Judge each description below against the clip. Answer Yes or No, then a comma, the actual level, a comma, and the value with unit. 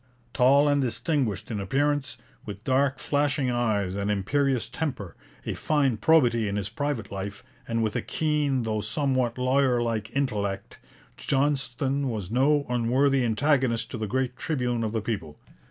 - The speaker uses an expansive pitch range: No, average, 4.3 semitones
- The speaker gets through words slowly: No, average, 155 wpm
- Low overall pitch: Yes, low, 125 Hz